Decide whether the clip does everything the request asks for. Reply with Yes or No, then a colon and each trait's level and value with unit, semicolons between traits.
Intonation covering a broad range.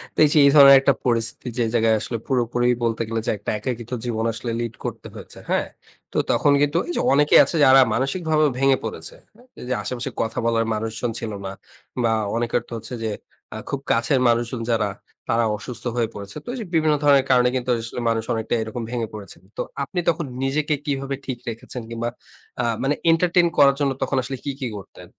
No: average, 3.3 semitones